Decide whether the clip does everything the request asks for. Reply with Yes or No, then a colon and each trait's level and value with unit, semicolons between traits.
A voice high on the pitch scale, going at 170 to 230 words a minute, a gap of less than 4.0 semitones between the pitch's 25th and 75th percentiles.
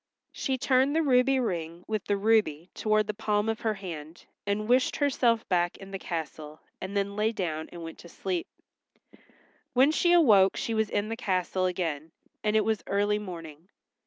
No: high, 205 Hz; average, 185 wpm; average, 4.3 semitones